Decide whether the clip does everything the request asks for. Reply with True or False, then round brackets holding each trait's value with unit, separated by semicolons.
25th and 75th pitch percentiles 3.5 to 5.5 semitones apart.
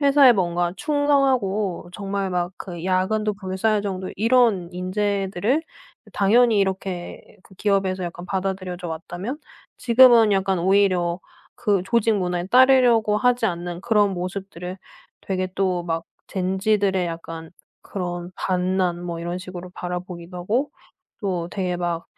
False (2.9 semitones)